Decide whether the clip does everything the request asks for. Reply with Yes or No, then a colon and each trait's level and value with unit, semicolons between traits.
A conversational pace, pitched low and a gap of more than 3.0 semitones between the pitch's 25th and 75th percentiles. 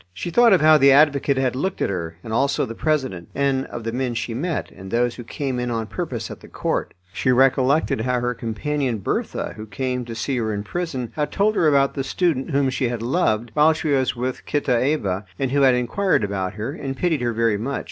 No: fast, 230 wpm; low, 130 Hz; average, 3.8 semitones